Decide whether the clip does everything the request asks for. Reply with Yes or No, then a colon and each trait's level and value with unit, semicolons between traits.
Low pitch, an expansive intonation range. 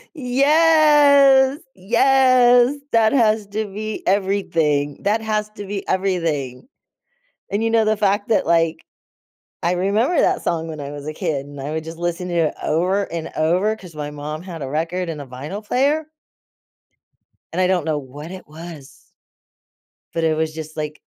No: medium, 180 Hz; wide, 5.8 semitones